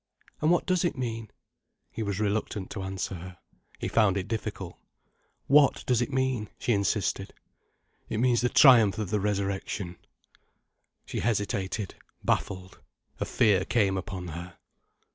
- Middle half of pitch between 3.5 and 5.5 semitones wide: Yes, average, 3.8 semitones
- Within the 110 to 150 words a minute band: Yes, average, 145 wpm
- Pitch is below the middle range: Yes, low, 105 Hz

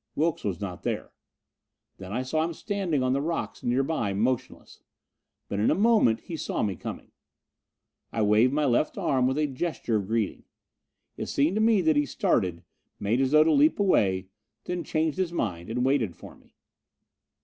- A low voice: Yes, low, 130 Hz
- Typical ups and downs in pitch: No, wide, 7.0 semitones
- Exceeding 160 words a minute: Yes, average, 180 wpm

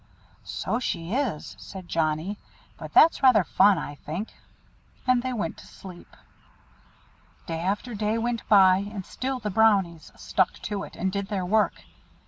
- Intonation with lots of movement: No, average, 3.7 semitones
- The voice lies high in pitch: Yes, high, 200 Hz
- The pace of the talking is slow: No, average, 155 wpm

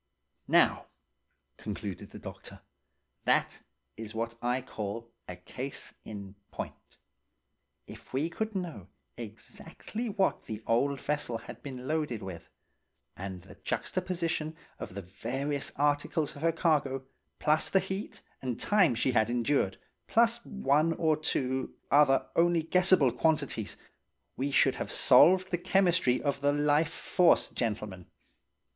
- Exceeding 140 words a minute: No, slow, 135 wpm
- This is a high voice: No, medium, 140 Hz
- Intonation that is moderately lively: No, wide, 6.2 semitones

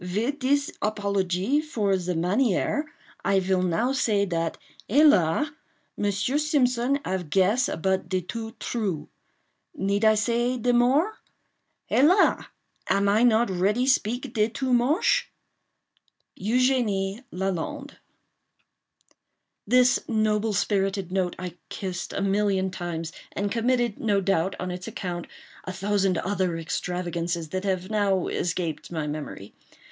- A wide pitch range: No, average, 4.8 semitones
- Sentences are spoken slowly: Yes, slow, 120 wpm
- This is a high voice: Yes, high, 200 Hz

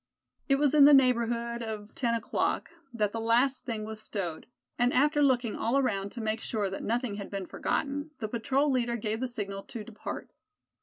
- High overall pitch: Yes, high, 235 Hz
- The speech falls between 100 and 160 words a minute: No, average, 195 wpm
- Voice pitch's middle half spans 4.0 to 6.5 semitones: No, average, 3.3 semitones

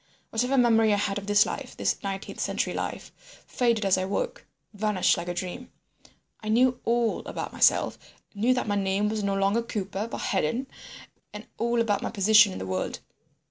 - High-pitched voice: Yes, high, 210 Hz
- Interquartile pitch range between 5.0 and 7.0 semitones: No, average, 2.9 semitones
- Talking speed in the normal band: Yes, average, 185 wpm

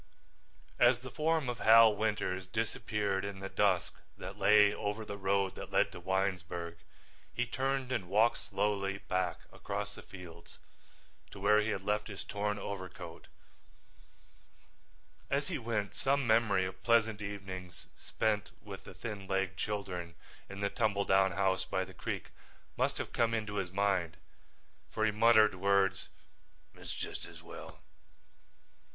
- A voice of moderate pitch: No, low, 100 Hz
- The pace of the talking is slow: No, average, 150 wpm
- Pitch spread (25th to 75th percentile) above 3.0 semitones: No, narrow, 2.5 semitones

